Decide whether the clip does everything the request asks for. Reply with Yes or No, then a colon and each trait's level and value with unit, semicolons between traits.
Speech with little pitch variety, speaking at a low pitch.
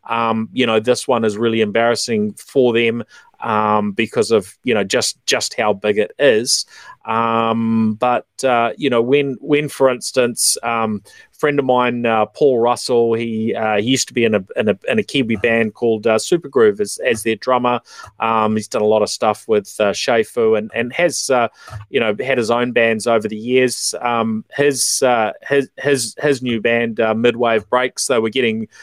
Yes: narrow, 2.1 semitones; low, 115 Hz